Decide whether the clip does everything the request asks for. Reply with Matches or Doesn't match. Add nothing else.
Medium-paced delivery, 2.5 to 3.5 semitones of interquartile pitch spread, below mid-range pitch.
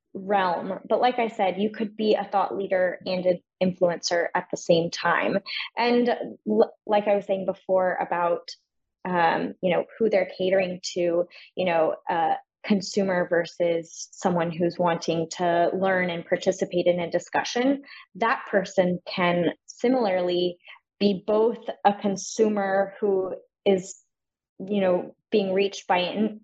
Doesn't match